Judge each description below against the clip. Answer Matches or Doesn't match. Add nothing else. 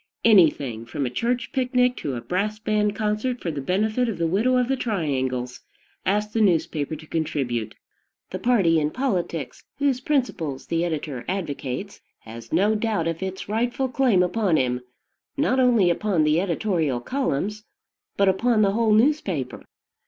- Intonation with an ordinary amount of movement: Doesn't match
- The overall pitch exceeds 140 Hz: Matches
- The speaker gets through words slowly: Doesn't match